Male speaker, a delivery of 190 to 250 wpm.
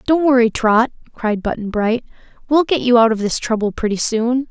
No: female; average, 200 wpm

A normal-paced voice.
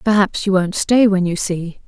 No: fast, 225 wpm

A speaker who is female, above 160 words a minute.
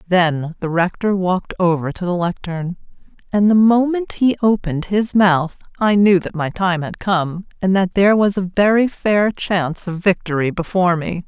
Yes: female; average, 180 wpm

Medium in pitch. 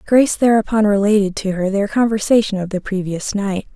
No: high, 205 Hz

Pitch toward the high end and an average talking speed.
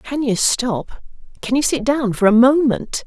Yes: very high, 250 Hz; average, 175 wpm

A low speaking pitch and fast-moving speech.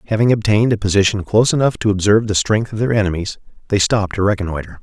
Yes: low, 105 Hz; fast, 210 wpm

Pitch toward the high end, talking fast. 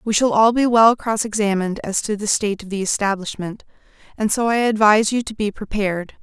Yes: high, 210 Hz; fast, 210 wpm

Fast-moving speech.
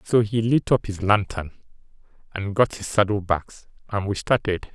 No: average, 175 wpm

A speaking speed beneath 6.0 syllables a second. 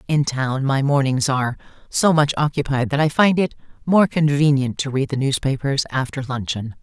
Yes: 5.0 syllables/s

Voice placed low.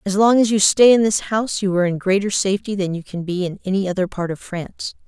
No: high, 195 Hz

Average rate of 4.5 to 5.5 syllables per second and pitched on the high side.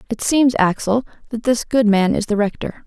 Yes: 5.1 syllables/s; high, 225 Hz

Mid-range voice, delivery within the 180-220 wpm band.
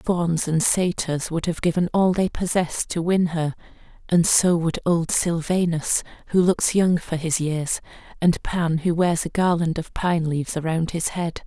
Yes: medium, 170 Hz; average, 190 wpm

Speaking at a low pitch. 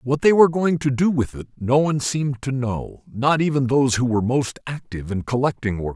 Yes: low, 130 Hz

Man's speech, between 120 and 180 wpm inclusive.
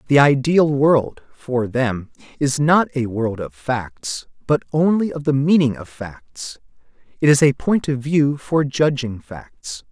Yes: male; average, 165 wpm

